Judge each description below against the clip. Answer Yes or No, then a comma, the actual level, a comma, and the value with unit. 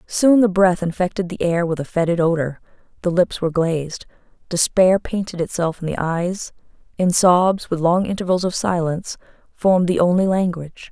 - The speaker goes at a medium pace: Yes, average, 170 wpm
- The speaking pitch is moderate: Yes, medium, 175 Hz